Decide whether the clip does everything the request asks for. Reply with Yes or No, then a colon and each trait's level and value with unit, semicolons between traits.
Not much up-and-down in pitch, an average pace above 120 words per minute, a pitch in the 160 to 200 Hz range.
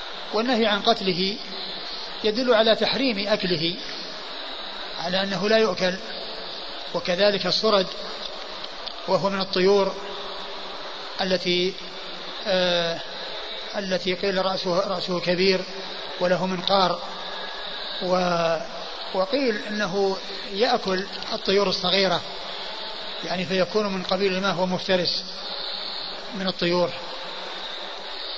No: narrow, 2.0 semitones; average, 80 wpm; high, 190 Hz